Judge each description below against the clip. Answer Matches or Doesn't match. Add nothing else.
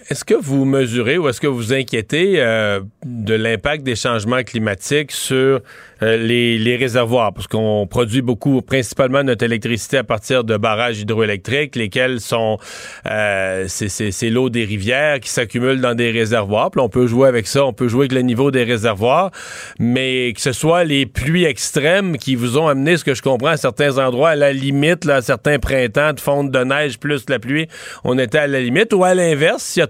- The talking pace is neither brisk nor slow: Matches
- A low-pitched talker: Matches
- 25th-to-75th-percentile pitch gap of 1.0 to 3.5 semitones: Matches